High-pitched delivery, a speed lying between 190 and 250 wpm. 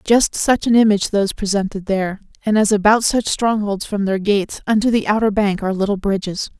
Yes: high, 205 Hz; average, 200 wpm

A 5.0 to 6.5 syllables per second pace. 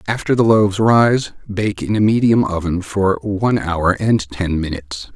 No: 4.5 syllables/s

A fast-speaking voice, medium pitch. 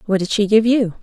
No: fast, 295 wpm; high, 210 Hz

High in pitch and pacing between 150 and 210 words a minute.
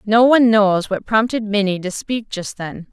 Yes: high, 210 Hz; fast, 205 wpm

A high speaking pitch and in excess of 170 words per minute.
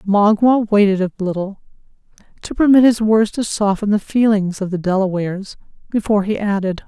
No: high, 205 Hz; average, 155 wpm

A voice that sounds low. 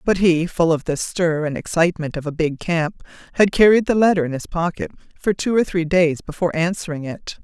No: medium, 170 Hz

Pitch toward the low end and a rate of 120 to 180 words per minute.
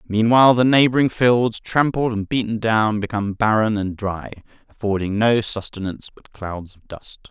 Yes: low, 110 Hz; average, 155 wpm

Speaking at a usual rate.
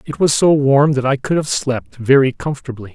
No: fast, 225 wpm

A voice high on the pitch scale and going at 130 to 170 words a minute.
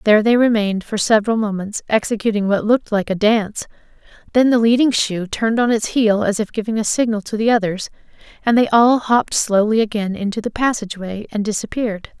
No: high, 215 Hz; average, 195 wpm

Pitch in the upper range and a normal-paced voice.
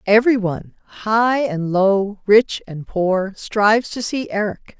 Yes: high, 210 Hz; average, 150 wpm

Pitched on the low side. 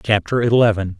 Yes: low, 110 Hz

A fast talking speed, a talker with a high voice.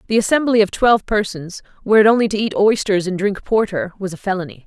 Yes: fast, 220 wpm; high, 200 Hz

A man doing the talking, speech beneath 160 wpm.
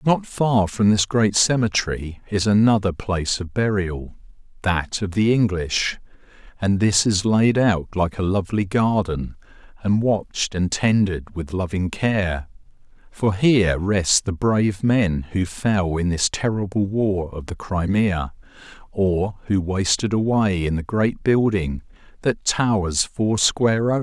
Yes: male; average, 150 wpm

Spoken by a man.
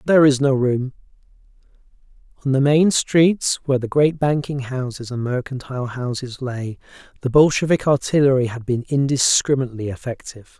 Yes: male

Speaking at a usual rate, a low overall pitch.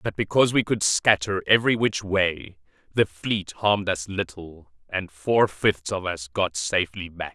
Yes: average, 170 wpm; very low, 95 Hz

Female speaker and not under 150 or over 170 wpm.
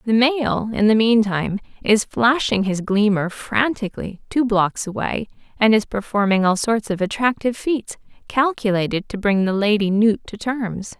Yes: female; average, 160 wpm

